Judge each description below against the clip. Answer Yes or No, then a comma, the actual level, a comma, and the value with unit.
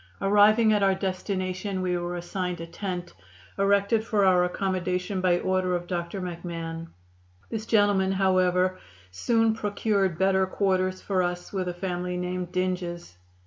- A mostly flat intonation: Yes, narrow, 1.8 semitones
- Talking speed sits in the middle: Yes, average, 145 wpm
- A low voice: No, medium, 185 Hz